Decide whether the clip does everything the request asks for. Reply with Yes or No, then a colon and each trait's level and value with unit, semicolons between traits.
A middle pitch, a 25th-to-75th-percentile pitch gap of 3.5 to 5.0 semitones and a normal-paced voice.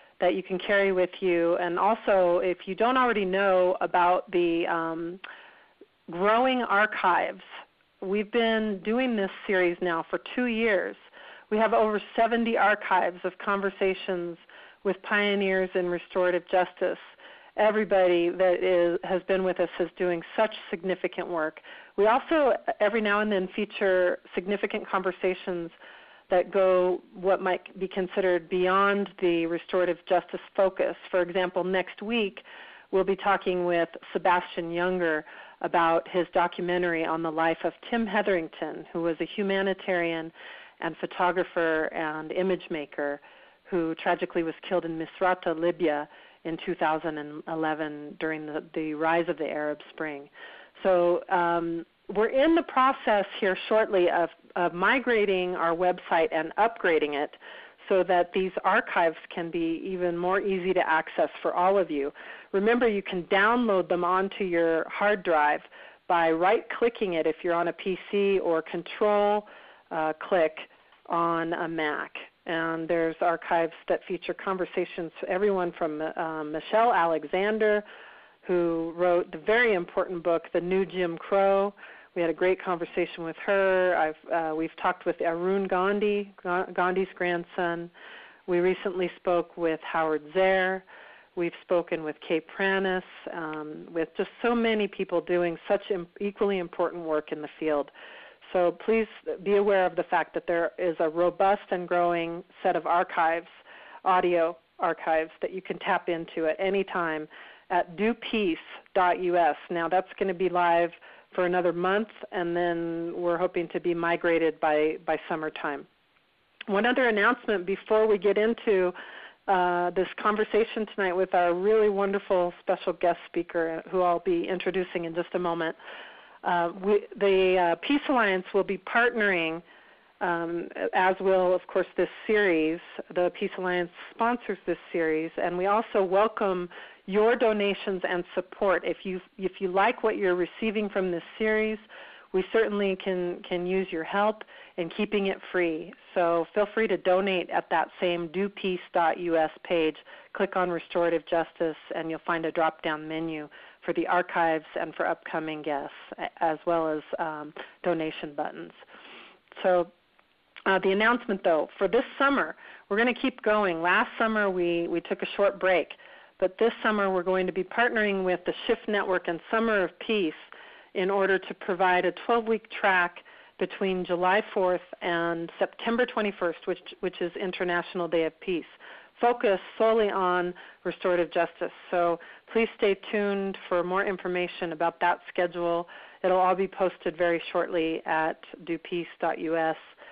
No: medium, 180 Hz; average, 2.8 semitones; average, 150 wpm